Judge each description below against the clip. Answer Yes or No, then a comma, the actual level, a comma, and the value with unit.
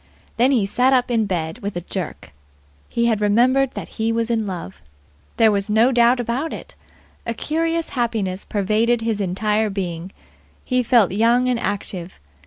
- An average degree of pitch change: Yes, average, 3.5 semitones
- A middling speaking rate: Yes, average, 170 wpm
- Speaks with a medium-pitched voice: No, high, 225 Hz